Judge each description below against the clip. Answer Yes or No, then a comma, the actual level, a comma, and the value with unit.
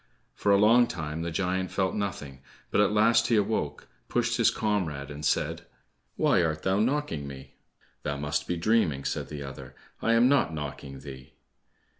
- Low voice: Yes, very low, 85 Hz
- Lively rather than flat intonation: Yes, wide, 6.5 semitones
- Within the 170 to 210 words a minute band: Yes, average, 175 wpm